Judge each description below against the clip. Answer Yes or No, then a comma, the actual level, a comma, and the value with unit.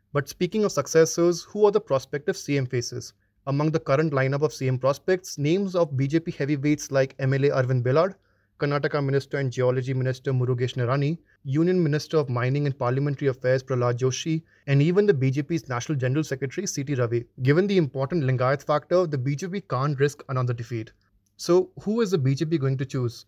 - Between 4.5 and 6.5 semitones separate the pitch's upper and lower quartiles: No, average, 3.8 semitones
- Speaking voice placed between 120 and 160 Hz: Yes, medium, 140 Hz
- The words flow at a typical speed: Yes, average, 180 wpm